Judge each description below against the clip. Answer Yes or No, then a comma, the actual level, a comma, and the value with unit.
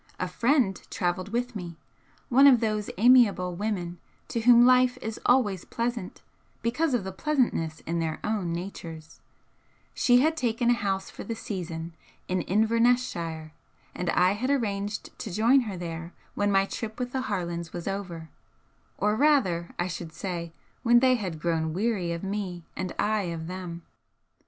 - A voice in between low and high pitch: No, high, 200 Hz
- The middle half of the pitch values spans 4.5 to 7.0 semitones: Yes, wide, 5.5 semitones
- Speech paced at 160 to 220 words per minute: Yes, average, 165 wpm